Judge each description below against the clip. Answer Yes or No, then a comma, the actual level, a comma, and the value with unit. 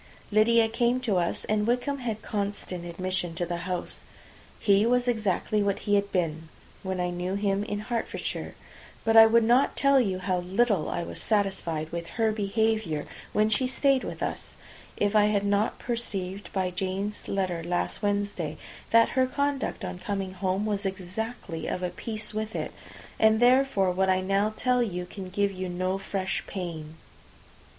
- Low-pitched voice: No, high, 200 Hz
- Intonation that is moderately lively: Yes, average, 3.3 semitones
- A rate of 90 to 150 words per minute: No, average, 175 wpm